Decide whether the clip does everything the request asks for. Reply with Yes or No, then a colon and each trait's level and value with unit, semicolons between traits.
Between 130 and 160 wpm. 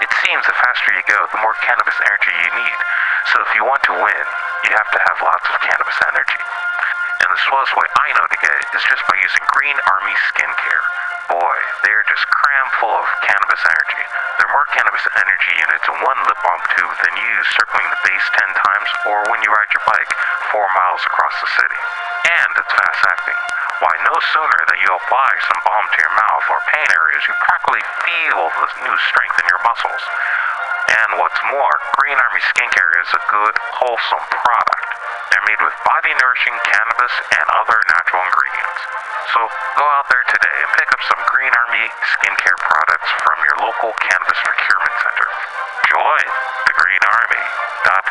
No: average, 190 wpm